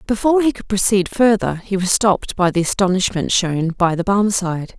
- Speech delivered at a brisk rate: No, average, 190 wpm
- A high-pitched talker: Yes, high, 195 Hz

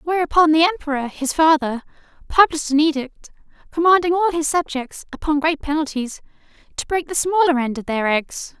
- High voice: Yes, very high, 305 Hz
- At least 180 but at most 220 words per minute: No, average, 160 wpm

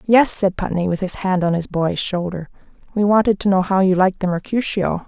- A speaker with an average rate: No, fast, 225 wpm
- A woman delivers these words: Yes, female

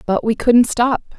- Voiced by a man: No, female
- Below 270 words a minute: Yes, average, 200 wpm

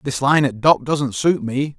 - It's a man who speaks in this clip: Yes, male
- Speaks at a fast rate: Yes, fast, 235 wpm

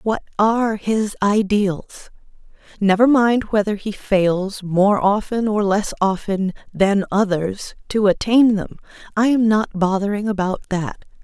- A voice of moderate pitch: No, high, 205 Hz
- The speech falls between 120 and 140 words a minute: Yes, slow, 135 wpm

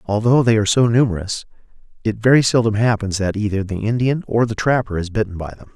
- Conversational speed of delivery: No, fast, 210 wpm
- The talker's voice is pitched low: Yes, low, 110 Hz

